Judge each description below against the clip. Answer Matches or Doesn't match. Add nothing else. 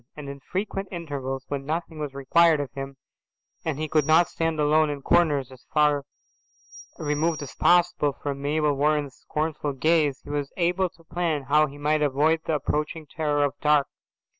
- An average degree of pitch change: Doesn't match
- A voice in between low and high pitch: Matches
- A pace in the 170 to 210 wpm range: Matches